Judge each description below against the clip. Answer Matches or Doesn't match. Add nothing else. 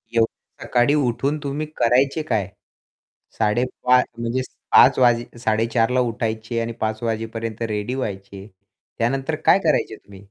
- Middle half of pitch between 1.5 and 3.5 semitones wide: Matches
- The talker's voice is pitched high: Doesn't match